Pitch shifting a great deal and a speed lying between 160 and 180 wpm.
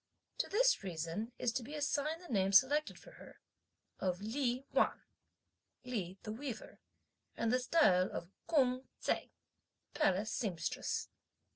No: wide, 6.7 semitones; slow, 135 wpm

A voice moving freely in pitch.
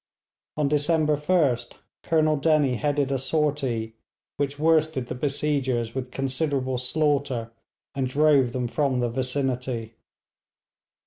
No: average, 3.0 semitones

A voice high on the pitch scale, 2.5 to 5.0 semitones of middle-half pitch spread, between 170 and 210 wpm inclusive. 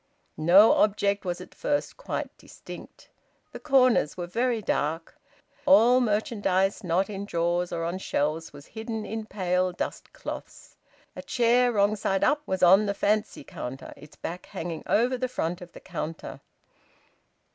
No: high, 200 Hz; average, 4.5 semitones; average, 155 wpm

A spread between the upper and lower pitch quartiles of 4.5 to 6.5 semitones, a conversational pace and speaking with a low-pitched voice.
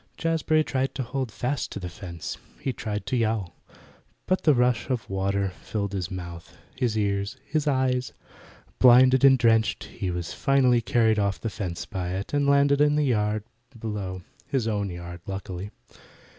Yes: average, 5.2 semitones; average, 170 wpm; low, 110 Hz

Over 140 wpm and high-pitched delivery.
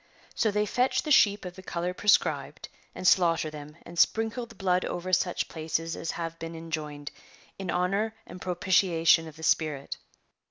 No: average, 170 wpm; medium, 175 Hz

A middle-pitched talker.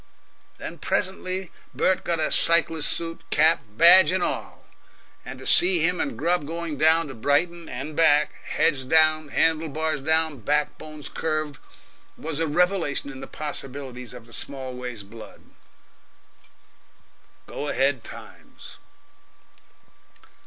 Yes: medium, 155 Hz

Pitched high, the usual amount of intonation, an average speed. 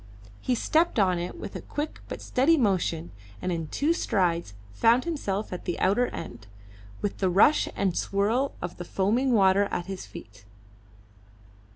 No: high, 195 Hz; wide, 5.9 semitones; average, 165 wpm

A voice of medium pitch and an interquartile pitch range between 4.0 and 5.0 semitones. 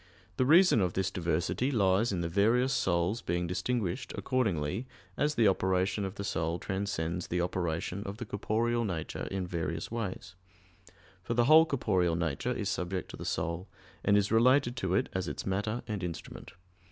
No: very low, 95 Hz; average, 4.7 semitones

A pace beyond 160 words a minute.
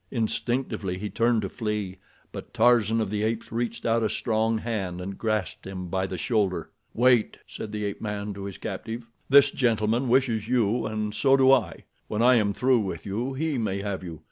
Yes: average, 195 wpm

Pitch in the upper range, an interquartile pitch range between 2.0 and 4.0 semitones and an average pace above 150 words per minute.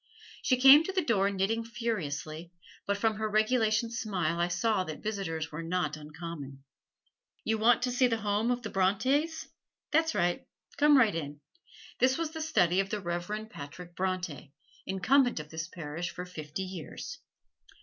No: high, 195 Hz; wide, 5.5 semitones; average, 165 wpm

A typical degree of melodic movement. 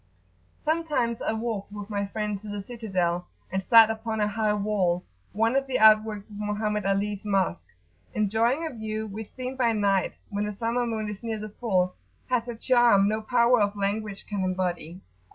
No: narrow, 2.3 semitones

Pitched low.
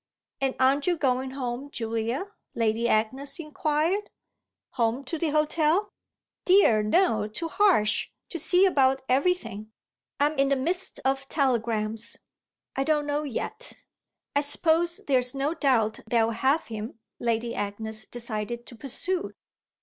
No: very high, 270 Hz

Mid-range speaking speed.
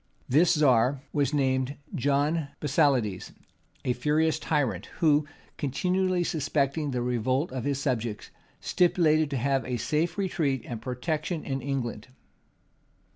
No: slow, 125 wpm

